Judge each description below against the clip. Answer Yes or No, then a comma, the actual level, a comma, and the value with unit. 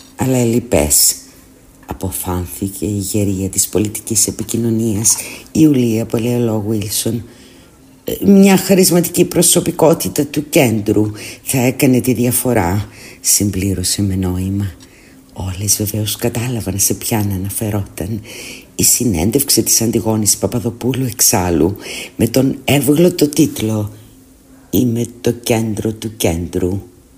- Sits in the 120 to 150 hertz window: No, low, 110 Hz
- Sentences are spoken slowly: Yes, slow, 100 wpm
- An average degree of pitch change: Yes, average, 3.8 semitones